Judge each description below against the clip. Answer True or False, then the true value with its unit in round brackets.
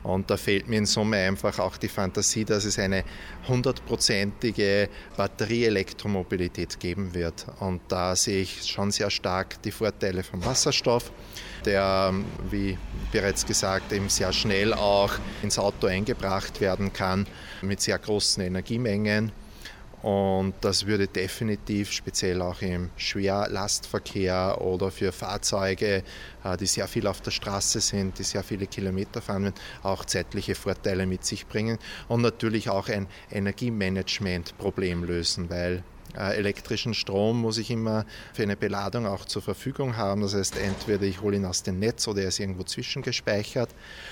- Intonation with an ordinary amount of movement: False (1.9 semitones)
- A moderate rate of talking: True (145 wpm)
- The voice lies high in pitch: False (100 Hz)